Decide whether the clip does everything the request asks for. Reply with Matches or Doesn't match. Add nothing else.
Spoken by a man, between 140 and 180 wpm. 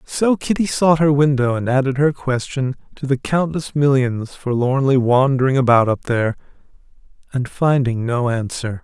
Matches